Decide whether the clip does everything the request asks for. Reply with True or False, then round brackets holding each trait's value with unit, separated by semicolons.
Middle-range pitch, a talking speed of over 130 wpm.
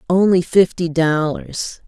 False (170 Hz; 95 wpm)